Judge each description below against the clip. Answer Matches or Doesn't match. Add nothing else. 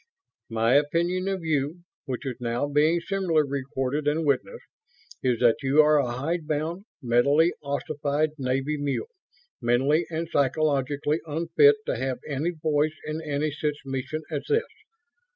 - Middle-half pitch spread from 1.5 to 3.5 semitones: Matches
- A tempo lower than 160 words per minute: Matches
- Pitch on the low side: Doesn't match